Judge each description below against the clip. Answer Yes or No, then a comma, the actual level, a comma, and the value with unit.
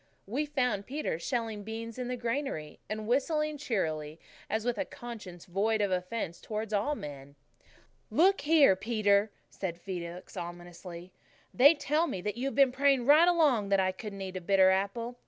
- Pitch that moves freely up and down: Yes, wide, 5.8 semitones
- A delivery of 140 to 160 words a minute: No, average, 170 wpm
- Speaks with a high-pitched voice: Yes, high, 215 Hz